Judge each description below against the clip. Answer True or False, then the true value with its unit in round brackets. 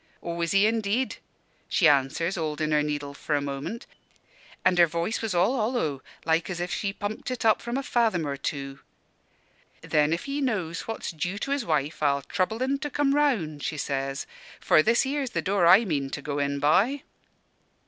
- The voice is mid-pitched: True (175 Hz)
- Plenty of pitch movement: True (7.3 semitones)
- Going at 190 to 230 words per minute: True (195 wpm)